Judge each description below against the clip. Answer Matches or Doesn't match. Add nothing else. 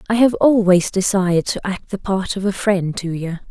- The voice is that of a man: Doesn't match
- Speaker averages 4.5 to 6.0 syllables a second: Matches